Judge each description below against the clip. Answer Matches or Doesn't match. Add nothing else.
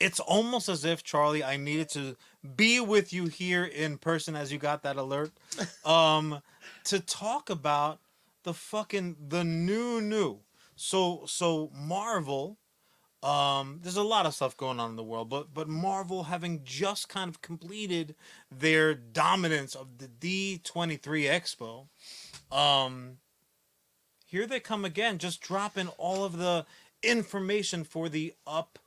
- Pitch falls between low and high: Matches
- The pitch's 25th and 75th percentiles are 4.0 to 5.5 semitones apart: Matches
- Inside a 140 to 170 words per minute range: Matches